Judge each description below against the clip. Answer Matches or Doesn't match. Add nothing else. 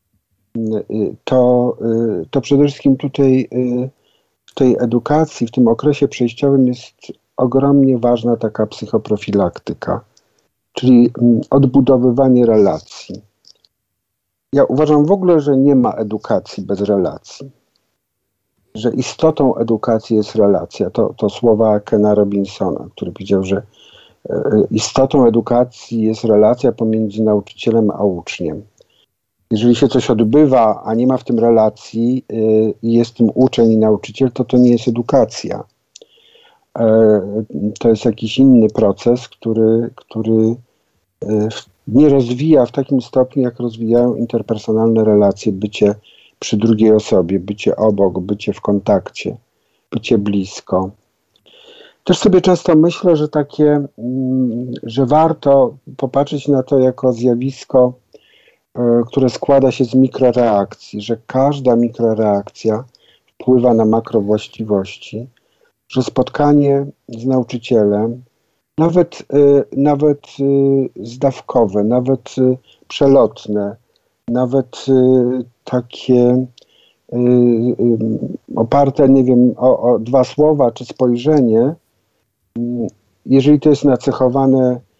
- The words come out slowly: Matches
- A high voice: Doesn't match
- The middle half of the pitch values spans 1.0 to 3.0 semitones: Doesn't match